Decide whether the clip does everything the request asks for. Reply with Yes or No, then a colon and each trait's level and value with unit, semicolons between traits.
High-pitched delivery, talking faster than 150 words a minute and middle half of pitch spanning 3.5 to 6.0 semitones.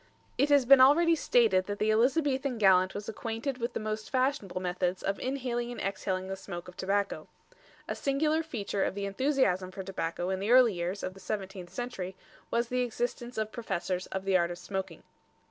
Yes: high, 210 Hz; average, 195 wpm; average, 4.9 semitones